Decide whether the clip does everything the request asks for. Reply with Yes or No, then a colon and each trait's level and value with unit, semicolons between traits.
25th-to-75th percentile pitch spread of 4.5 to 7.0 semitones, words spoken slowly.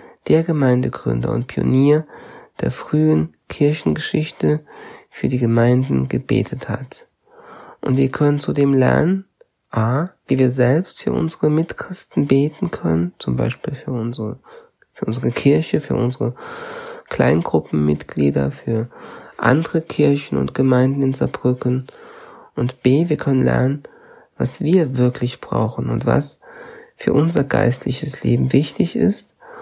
Yes: wide, 5.5 semitones; slow, 120 wpm